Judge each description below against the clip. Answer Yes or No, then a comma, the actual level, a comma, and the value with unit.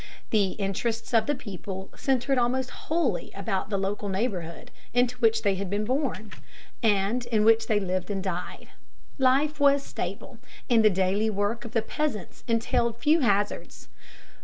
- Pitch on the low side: No, high, 220 Hz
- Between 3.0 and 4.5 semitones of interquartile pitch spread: Yes, average, 3.9 semitones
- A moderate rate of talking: Yes, average, 160 wpm